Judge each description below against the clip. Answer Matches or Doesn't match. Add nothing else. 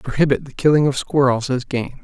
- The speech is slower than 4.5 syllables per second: Doesn't match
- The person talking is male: Matches